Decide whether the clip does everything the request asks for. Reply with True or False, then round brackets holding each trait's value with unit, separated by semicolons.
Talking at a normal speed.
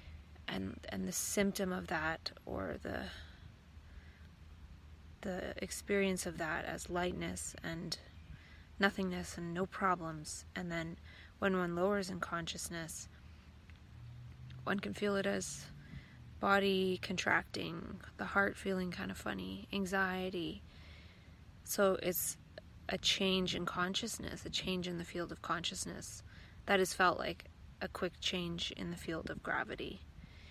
False (130 wpm)